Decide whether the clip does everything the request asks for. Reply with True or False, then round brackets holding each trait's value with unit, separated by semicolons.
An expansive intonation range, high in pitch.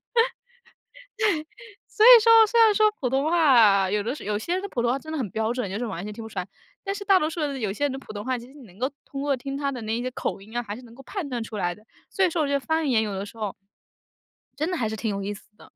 True (6.5 semitones; 250 Hz)